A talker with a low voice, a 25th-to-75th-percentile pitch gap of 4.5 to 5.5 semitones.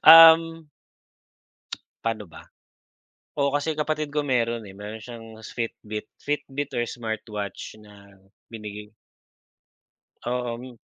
Yes: low, 120 Hz; average, 5.2 semitones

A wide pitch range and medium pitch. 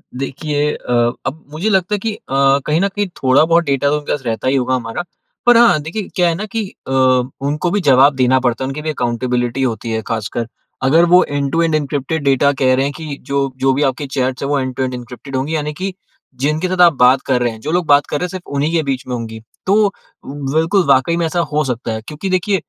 No: average, 4.3 semitones; medium, 145 Hz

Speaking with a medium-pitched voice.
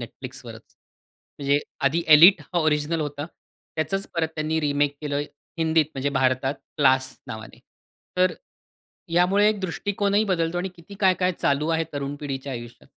Yes: medium, 155 Hz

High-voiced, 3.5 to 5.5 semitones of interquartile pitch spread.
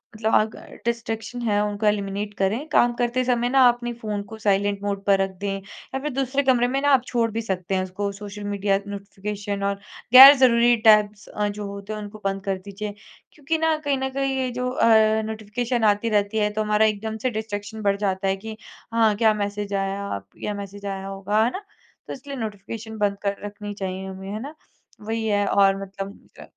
No: high, 210 Hz; average, 2.8 semitones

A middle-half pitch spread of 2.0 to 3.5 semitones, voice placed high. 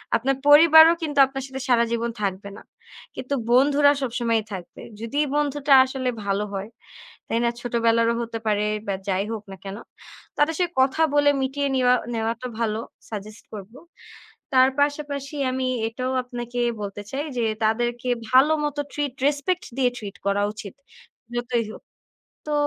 No: average, 4.1 semitones; high, 245 Hz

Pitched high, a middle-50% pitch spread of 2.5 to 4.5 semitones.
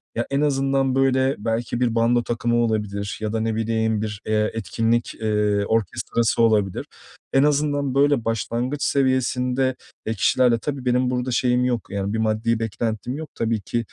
No: low, 115 Hz; average, 2.8 semitones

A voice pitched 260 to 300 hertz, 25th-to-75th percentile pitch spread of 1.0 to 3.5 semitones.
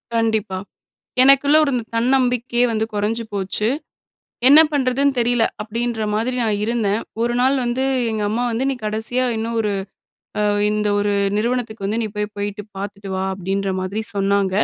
No: high, 220 Hz; average, 3.0 semitones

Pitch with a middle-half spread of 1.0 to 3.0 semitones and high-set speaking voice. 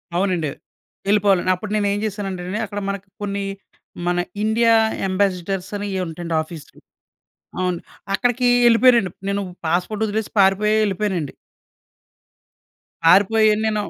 Yes: average, 2.7 semitones; high, 200 Hz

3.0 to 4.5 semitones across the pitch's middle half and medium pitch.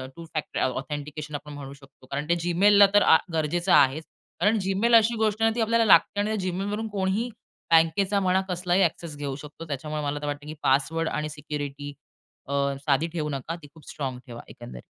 No: average, 5.0 semitones; medium, 160 Hz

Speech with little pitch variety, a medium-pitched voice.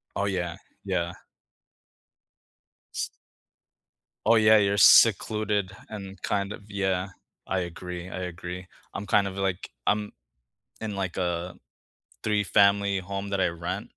No: narrow, 2.0 semitones; very low, 95 Hz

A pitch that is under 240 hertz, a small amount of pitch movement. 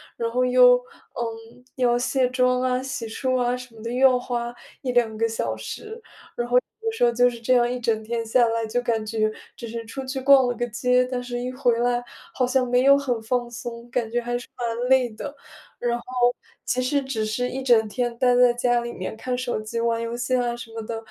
No: high, 245 Hz; narrow, 1.5 semitones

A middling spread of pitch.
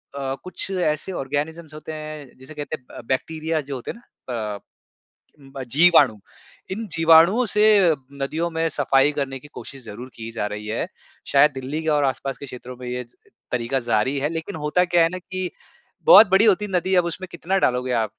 Yes: average, 4.5 semitones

